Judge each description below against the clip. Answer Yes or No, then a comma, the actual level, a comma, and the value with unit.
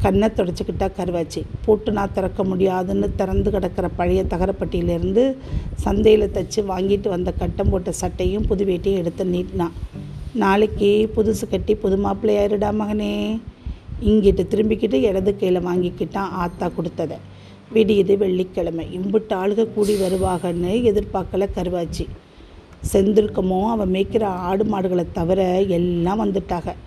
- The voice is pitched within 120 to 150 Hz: No, high, 195 Hz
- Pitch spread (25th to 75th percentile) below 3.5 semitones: Yes, narrow, 2.5 semitones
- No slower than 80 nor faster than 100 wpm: No, average, 110 wpm